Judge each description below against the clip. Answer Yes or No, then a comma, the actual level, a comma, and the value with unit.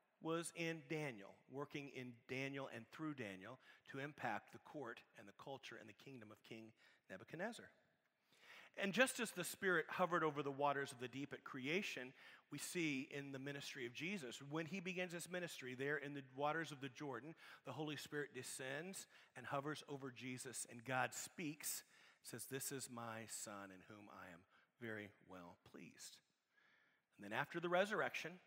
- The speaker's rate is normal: Yes, average, 175 wpm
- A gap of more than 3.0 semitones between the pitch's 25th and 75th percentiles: Yes, average, 4.1 semitones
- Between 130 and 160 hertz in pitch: Yes, medium, 140 Hz